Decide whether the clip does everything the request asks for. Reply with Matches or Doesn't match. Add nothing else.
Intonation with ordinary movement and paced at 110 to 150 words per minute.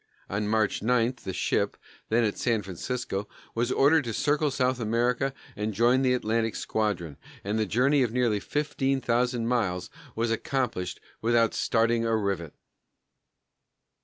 Matches